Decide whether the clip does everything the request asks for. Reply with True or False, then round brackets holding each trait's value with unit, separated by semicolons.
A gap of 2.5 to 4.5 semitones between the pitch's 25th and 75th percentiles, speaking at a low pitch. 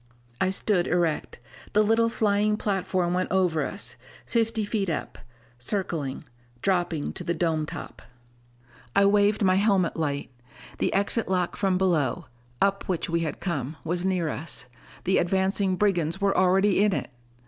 False (3.0 semitones; 185 Hz)